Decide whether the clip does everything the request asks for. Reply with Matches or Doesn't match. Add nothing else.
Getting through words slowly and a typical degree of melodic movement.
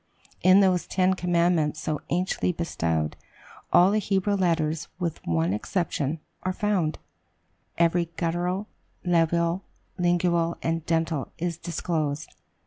Doesn't match